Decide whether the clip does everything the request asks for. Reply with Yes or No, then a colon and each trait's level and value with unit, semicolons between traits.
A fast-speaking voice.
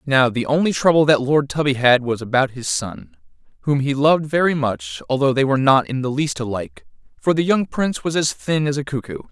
Yes: fast, 225 wpm